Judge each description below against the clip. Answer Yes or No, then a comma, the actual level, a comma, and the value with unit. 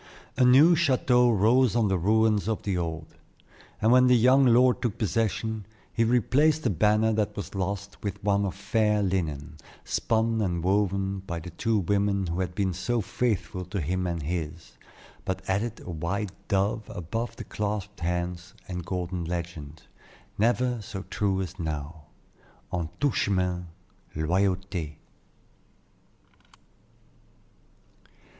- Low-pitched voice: Yes, low, 100 Hz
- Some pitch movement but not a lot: Yes, average, 4.0 semitones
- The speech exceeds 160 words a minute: No, average, 140 wpm